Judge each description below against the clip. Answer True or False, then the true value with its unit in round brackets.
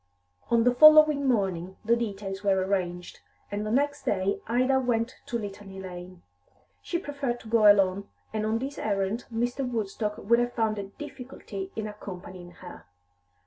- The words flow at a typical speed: True (160 wpm)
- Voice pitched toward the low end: False (215 Hz)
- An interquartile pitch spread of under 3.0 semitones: False (4.0 semitones)